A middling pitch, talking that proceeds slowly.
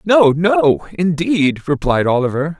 Yes: medium, 160 Hz; slow, 115 wpm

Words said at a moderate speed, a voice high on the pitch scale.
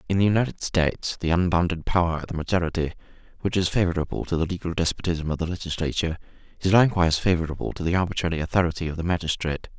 No: average, 185 wpm; very low, 85 Hz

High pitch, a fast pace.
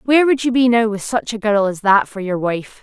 Yes: high, 225 Hz; fast, 300 wpm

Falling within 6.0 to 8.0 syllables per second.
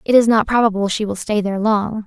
Yes: 6.1 syllables/s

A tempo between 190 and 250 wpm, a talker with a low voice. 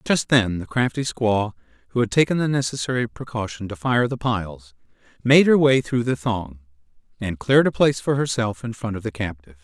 Yes: average, 200 wpm; low, 115 Hz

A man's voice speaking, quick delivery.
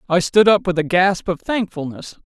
Yes: male; fast, 210 wpm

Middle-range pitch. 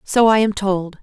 No: high, 200 Hz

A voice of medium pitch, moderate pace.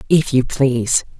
No: low, 130 Hz; average, 150 wpm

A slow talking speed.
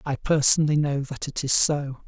No: fast, 205 wpm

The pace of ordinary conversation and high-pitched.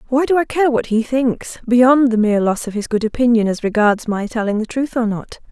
No: fast, 250 wpm; high, 235 Hz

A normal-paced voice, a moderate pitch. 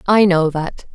Yes: average, 190 wpm; medium, 180 Hz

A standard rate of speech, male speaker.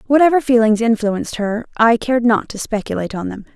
No: average, 185 wpm; female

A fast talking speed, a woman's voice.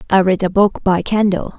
Yes: fast, 230 wpm; female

